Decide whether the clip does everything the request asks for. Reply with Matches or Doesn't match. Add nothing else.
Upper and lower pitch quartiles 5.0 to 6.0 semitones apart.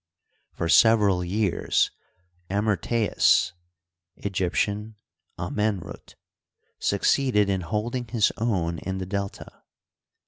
Doesn't match